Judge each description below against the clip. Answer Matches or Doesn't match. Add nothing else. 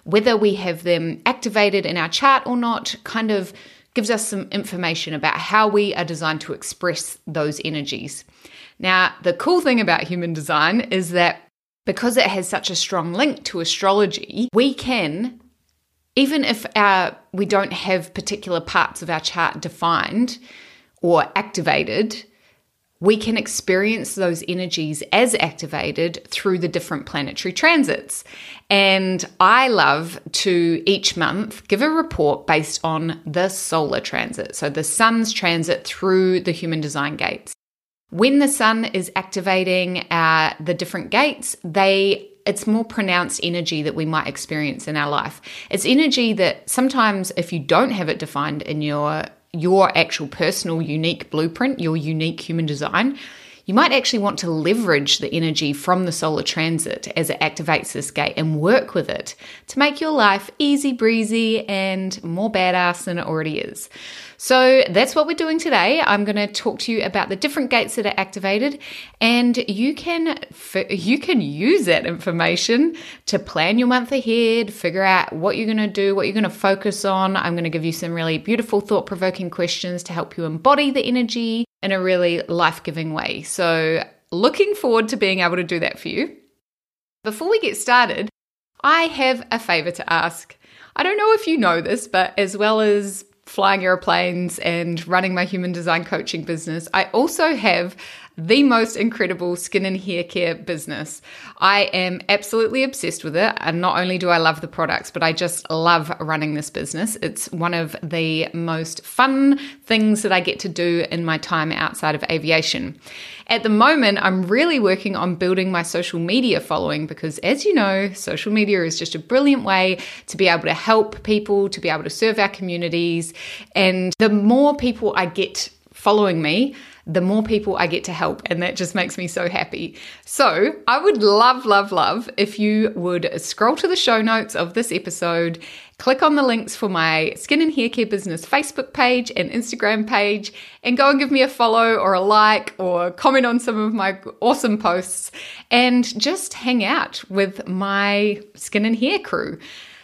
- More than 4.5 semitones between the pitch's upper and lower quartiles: Matches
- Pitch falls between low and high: Doesn't match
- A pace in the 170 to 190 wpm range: Matches